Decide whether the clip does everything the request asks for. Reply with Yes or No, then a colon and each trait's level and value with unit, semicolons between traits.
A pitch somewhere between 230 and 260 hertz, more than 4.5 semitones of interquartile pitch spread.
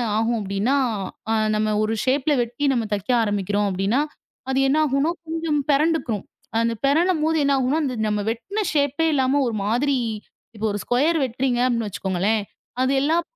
Yes: very high, 255 Hz; average, 5.1 semitones